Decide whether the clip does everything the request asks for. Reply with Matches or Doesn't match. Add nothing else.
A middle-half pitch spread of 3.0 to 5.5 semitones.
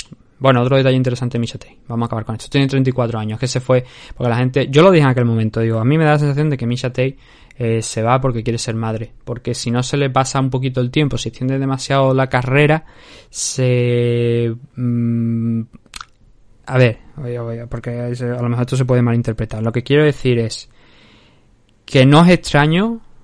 Doesn't match